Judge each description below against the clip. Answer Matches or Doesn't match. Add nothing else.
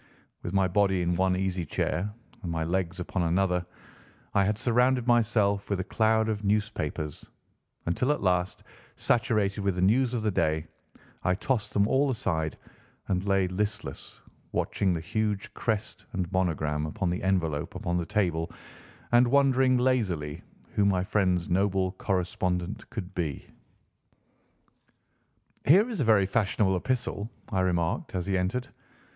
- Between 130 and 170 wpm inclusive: Matches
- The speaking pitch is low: Matches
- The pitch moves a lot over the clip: Doesn't match